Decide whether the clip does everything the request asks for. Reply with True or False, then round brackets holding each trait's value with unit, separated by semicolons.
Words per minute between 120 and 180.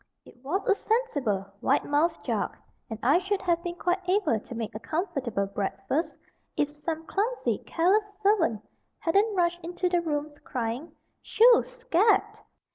True (150 wpm)